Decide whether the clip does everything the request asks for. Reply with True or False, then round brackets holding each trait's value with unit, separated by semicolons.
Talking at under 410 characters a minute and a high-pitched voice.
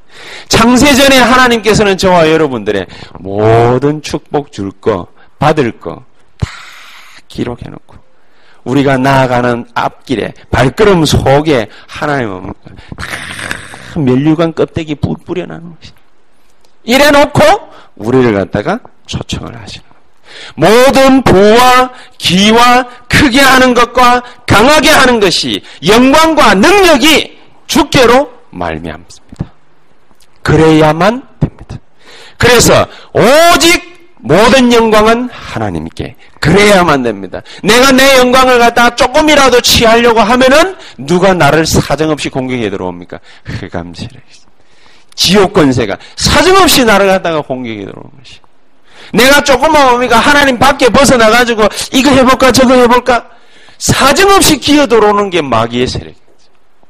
True (265 characters per minute; 215 Hz)